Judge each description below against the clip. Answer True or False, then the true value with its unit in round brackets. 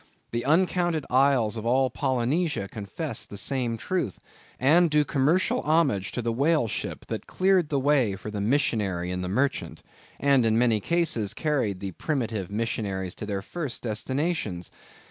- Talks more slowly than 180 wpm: True (160 wpm)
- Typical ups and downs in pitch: False (6.2 semitones)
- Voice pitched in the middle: False (125 Hz)